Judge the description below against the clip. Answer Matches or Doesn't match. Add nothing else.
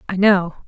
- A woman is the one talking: Matches